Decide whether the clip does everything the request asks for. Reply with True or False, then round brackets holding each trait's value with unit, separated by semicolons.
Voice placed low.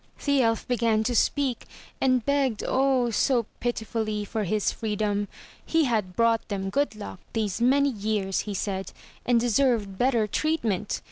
False (225 Hz)